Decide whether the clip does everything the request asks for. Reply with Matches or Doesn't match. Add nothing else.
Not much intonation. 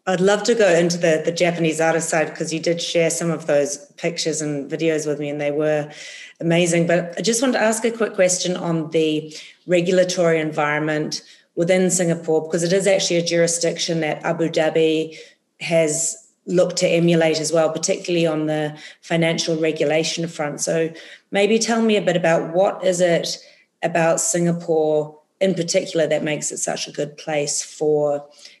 Matches